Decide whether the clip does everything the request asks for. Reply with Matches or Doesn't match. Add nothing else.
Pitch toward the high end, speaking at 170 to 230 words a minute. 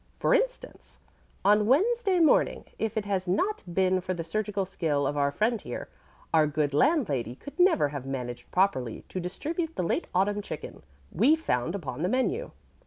Matches